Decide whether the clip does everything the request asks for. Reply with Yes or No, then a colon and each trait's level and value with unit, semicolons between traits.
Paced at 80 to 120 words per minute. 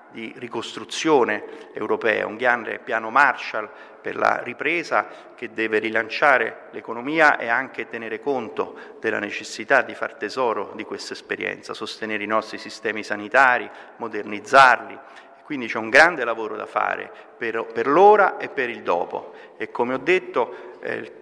No: average, 145 wpm